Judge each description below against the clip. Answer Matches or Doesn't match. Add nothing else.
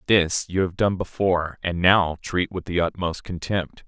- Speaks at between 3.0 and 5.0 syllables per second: Matches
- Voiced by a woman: Doesn't match